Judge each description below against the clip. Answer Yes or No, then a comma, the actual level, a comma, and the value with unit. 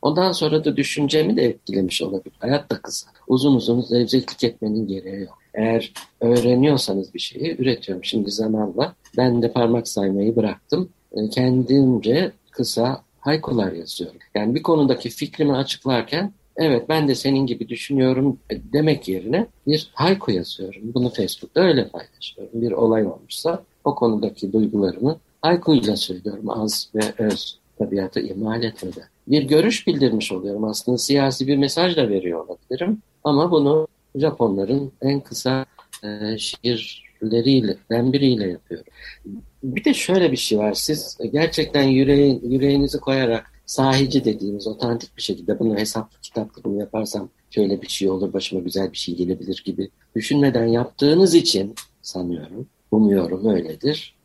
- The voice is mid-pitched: No, low, 120 Hz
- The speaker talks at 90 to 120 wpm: No, average, 135 wpm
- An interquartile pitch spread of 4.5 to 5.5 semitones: Yes, average, 4.8 semitones